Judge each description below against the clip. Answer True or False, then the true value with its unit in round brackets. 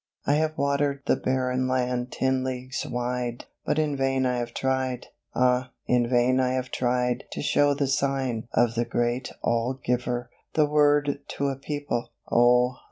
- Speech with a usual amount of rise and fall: False (2.0 semitones)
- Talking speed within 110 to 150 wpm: False (165 wpm)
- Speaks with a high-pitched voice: False (130 Hz)